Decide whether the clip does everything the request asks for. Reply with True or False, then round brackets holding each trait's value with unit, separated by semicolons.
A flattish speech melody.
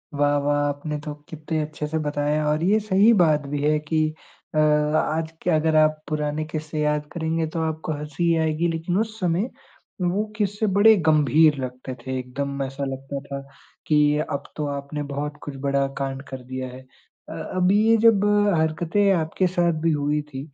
True (2.3 semitones)